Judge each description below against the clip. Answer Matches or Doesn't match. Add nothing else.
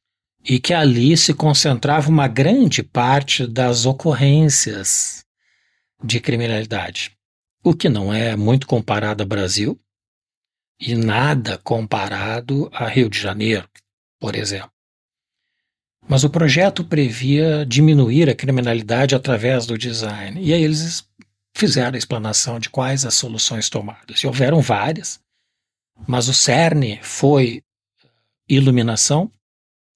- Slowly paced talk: Matches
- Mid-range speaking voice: Doesn't match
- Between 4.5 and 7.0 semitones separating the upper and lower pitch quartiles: Matches